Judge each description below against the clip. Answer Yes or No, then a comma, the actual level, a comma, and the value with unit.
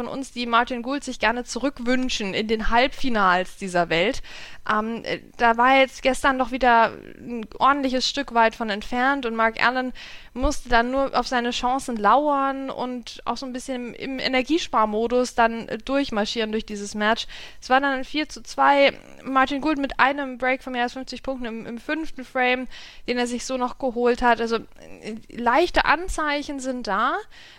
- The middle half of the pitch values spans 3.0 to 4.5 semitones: No, narrow, 2.6 semitones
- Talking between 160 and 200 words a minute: Yes, average, 175 wpm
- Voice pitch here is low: No, very high, 250 Hz